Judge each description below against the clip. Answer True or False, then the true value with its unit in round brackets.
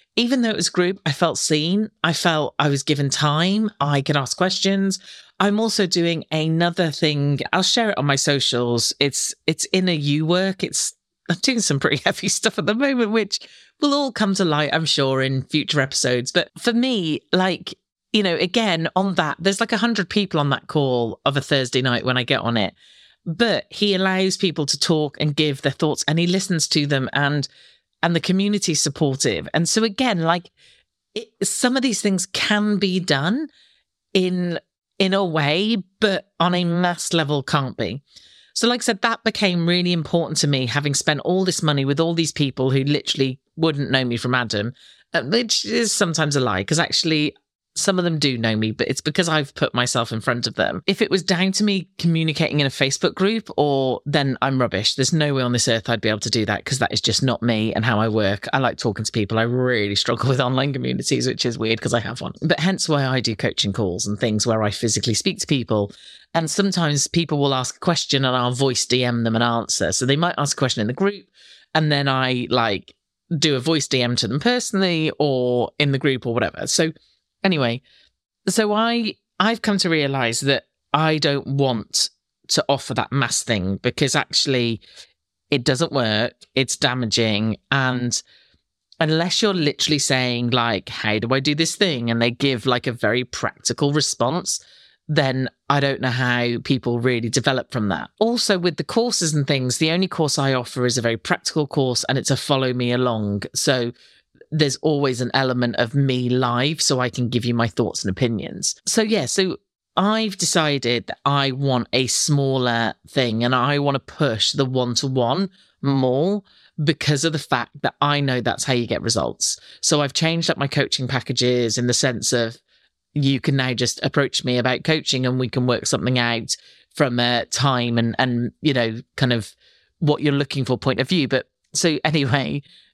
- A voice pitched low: False (145 Hz)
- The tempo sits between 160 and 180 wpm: False (205 wpm)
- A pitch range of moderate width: False (5.7 semitones)